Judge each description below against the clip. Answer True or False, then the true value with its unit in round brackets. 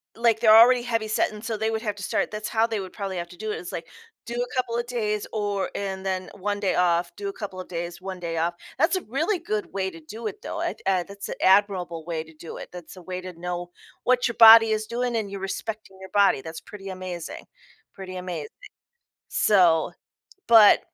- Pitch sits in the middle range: False (200 Hz)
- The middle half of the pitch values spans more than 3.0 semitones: True (3.5 semitones)